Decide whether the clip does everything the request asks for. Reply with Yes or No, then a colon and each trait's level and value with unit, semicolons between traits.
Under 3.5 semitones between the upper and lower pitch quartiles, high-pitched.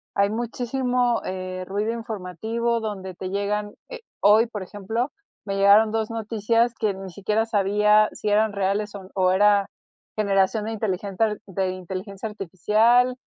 Yes: narrow, 2.5 semitones; high, 210 Hz